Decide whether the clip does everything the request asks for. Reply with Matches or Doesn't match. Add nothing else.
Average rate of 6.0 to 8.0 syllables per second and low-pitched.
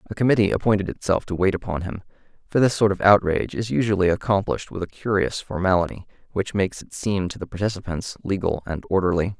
Matches